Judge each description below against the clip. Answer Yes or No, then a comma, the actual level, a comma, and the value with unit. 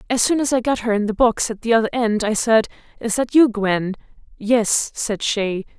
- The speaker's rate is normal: No, fast, 230 wpm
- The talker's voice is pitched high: Yes, high, 225 Hz